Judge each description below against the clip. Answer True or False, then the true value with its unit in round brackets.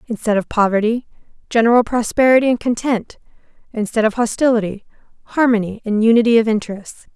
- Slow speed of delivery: True (125 wpm)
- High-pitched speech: True (225 Hz)